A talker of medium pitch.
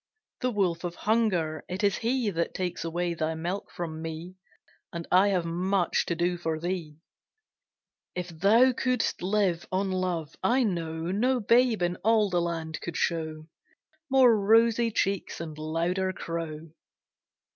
Yes: medium, 180 Hz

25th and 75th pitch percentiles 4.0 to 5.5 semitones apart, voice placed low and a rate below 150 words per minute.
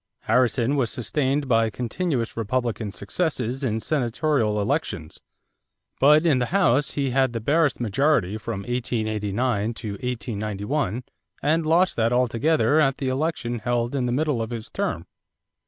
Yes: average, 4.3 semitones; low, 125 Hz; average, 140 wpm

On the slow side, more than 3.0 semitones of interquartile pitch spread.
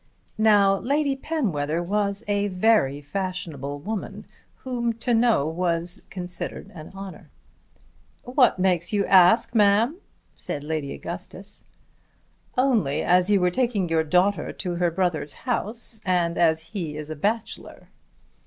Yes: slow, 130 wpm; average, 4.7 semitones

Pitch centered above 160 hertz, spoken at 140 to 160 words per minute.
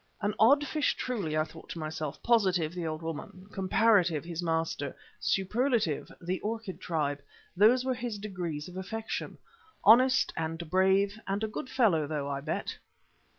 Yes: medium, 185 Hz; average, 155 wpm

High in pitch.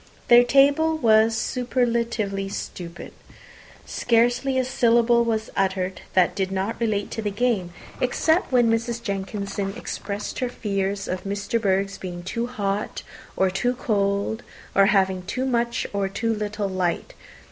Yes: high, 215 Hz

